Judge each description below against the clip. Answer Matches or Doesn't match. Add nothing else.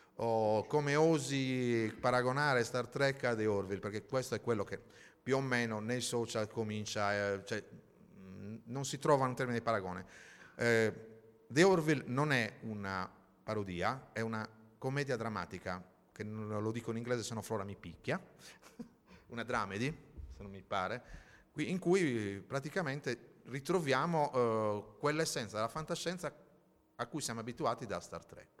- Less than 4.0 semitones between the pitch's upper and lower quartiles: Doesn't match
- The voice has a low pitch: Matches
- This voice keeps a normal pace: Matches